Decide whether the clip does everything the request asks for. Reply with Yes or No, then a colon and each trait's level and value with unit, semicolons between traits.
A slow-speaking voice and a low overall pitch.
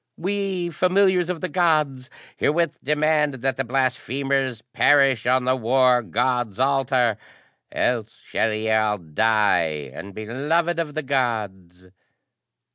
Yes: slow, 120 wpm; low, 130 Hz